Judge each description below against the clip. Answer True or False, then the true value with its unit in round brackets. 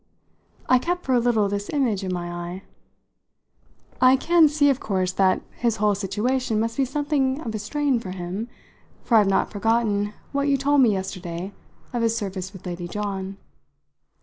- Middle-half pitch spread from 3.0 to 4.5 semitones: False (5.4 semitones)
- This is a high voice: True (215 Hz)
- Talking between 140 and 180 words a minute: True (175 wpm)